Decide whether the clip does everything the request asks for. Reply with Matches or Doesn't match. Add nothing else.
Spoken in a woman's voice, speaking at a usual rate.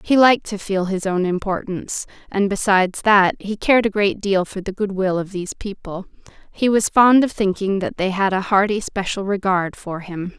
Doesn't match